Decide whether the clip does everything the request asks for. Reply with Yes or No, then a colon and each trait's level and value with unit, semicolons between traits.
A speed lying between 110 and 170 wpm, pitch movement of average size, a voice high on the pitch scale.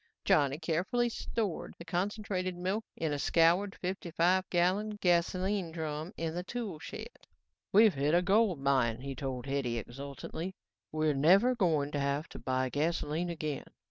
No: average, 155 wpm; average, 4.8 semitones; medium, 170 Hz